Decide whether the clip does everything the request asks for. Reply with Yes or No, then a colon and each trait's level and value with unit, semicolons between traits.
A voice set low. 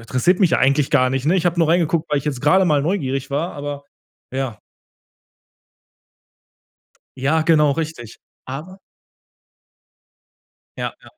No: medium, 150 Hz